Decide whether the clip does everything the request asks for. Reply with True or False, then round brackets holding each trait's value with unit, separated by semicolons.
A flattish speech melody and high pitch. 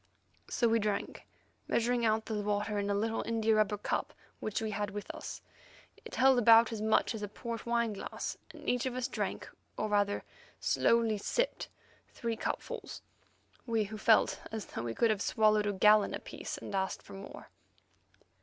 True (1.8 semitones; 215 Hz)